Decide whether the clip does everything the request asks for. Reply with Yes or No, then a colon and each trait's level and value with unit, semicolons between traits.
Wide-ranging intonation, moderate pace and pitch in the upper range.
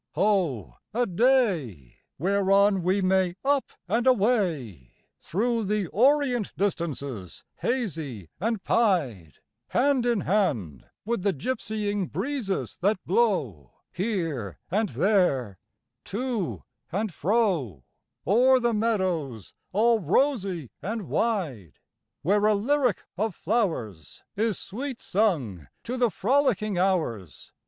No: wide, 6.6 semitones; slow, 110 wpm; high, 195 Hz